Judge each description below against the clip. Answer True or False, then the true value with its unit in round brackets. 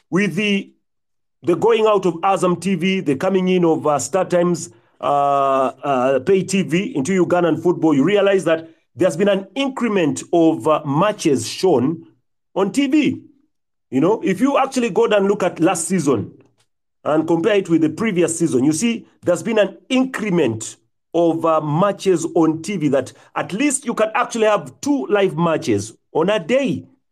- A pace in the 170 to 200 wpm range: True (175 wpm)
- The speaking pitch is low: False (185 Hz)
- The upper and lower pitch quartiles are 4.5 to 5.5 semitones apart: True (4.8 semitones)